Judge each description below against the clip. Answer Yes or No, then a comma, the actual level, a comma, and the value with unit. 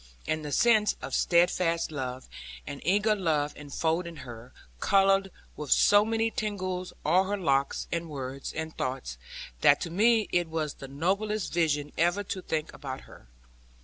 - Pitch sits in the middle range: Yes, medium, 170 Hz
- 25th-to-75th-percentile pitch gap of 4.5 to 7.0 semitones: Yes, average, 5.1 semitones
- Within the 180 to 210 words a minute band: No, average, 155 wpm